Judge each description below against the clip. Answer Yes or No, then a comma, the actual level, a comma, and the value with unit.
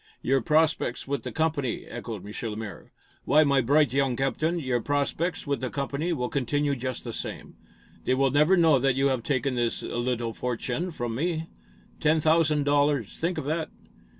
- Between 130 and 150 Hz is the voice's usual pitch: Yes, medium, 140 Hz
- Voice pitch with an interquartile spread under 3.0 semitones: No, average, 3.7 semitones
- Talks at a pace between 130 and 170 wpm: No, average, 180 wpm